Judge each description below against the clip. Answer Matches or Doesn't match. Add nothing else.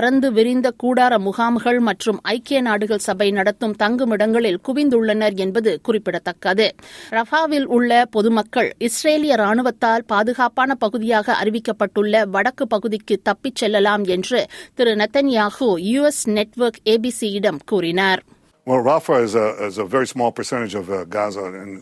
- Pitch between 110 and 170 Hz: Doesn't match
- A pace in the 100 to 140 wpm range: Doesn't match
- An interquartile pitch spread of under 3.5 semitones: Matches